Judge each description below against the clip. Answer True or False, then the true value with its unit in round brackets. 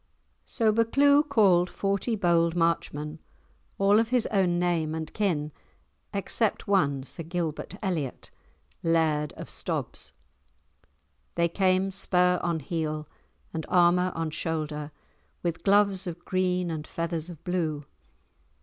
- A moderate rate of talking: False (120 wpm)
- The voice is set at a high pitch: False (175 Hz)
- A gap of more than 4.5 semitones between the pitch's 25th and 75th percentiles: False (3.5 semitones)